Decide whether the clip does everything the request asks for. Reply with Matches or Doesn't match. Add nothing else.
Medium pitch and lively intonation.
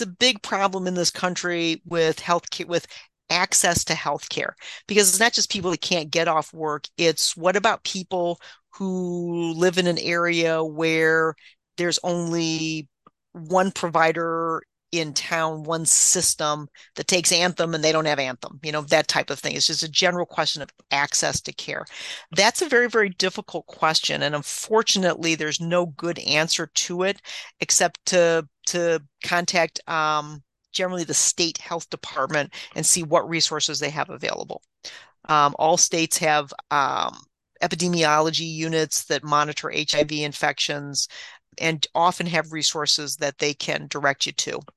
Doesn't match